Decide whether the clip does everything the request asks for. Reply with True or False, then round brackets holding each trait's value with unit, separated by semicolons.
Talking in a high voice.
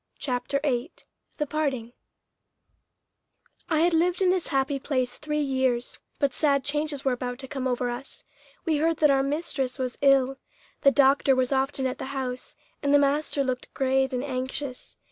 True (275 Hz)